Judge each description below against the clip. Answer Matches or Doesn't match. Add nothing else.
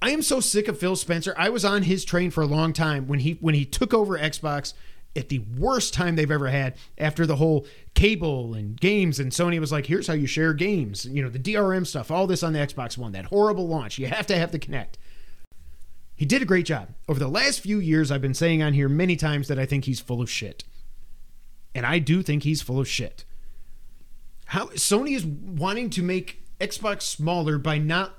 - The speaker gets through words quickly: Matches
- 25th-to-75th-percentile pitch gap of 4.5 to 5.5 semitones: Matches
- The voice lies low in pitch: Doesn't match